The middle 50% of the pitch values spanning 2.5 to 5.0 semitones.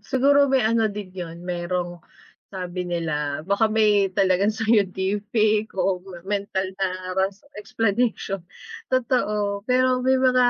Yes: average, 3.3 semitones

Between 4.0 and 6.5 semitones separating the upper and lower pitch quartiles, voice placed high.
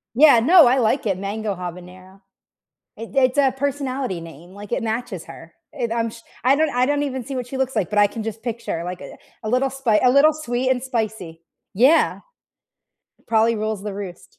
Yes: average, 4.6 semitones; high, 230 Hz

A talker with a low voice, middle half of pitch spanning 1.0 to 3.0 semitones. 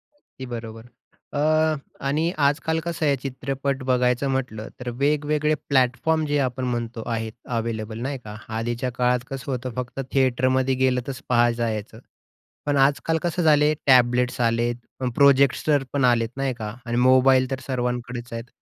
Yes: low, 130 Hz; average, 2.7 semitones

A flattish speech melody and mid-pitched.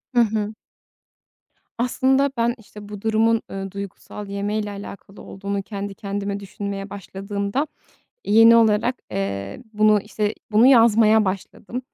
No: narrow, 2.1 semitones; high, 210 Hz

